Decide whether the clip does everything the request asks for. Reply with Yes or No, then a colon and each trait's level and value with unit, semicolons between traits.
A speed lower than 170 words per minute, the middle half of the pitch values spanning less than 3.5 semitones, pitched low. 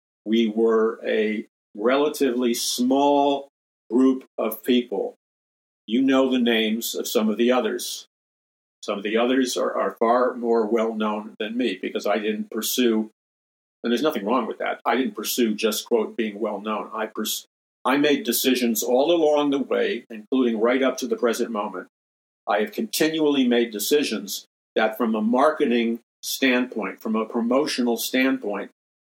Yes: average, 160 wpm; average, 3.1 semitones; low, 120 Hz